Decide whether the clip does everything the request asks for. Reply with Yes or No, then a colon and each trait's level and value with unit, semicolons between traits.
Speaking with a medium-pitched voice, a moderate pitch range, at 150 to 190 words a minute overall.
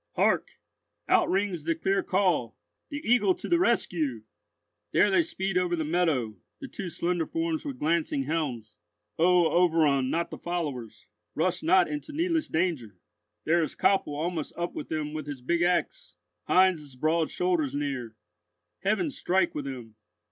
Yes: medium, 170 Hz; average, 4.2 semitones; average, 155 wpm